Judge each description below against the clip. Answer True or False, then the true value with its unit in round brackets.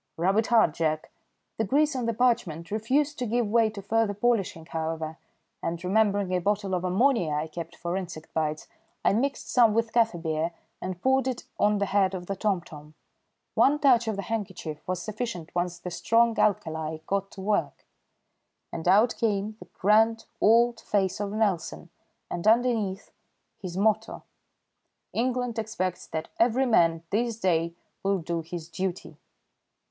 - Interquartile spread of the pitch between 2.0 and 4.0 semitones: False (4.8 semitones)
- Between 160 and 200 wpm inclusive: True (165 wpm)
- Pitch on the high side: True (200 Hz)